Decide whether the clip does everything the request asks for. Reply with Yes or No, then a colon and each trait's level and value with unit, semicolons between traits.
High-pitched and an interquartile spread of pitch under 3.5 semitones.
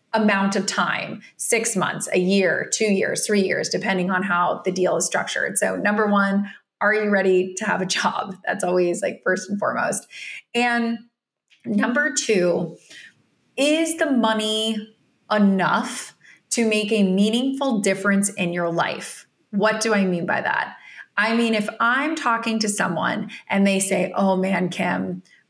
Yes: high, 205 Hz; average, 3.0 semitones